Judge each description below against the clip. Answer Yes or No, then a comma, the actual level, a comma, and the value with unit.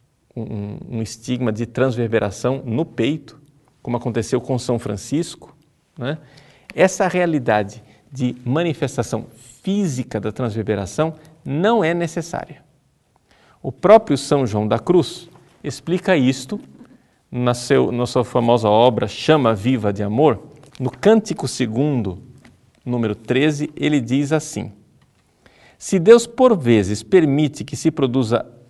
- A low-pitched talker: Yes, low, 130 Hz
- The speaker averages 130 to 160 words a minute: No, slow, 120 wpm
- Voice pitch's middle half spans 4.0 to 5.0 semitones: Yes, average, 4.7 semitones